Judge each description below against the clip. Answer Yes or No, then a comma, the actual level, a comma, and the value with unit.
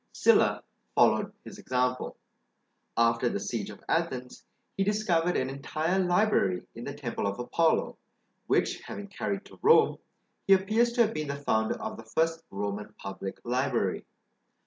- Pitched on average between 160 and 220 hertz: No, medium, 140 Hz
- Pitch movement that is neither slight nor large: No, wide, 8.5 semitones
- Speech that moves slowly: No, average, 150 wpm